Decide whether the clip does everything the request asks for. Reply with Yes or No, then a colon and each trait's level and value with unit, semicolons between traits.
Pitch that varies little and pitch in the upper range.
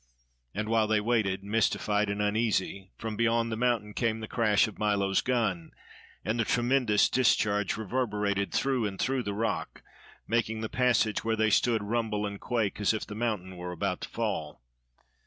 No: narrow, 2.3 semitones; low, 110 Hz